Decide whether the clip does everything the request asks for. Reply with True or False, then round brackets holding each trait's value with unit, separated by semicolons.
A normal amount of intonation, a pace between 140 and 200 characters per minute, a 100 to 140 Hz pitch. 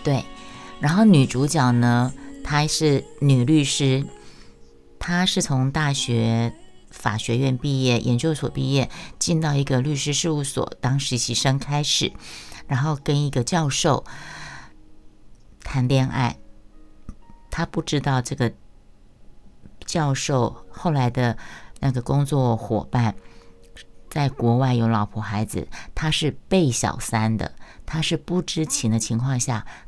True (3.7 semitones; 185 characters per minute; 135 Hz)